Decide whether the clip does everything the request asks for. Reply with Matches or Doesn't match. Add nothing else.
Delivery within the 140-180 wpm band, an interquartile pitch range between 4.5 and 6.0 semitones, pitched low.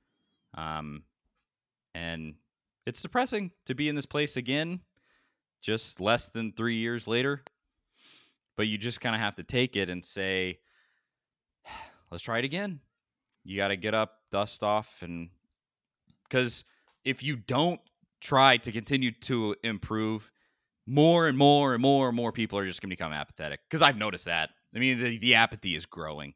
Matches